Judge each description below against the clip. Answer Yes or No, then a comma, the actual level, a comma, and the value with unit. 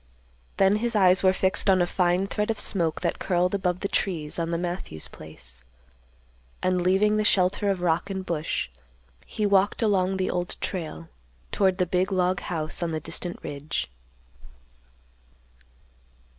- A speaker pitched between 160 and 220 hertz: Yes, medium, 185 Hz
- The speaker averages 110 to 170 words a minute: Yes, average, 155 wpm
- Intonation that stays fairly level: Yes, narrow, 2.2 semitones